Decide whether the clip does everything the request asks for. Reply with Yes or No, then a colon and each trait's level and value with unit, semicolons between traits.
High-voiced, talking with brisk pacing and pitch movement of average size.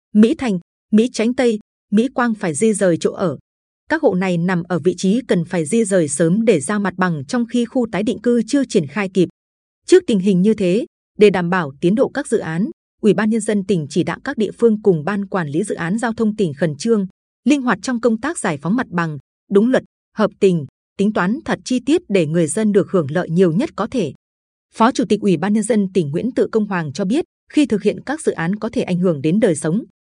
Yes: high, 205 Hz; fast, 255 wpm; average, 4.2 semitones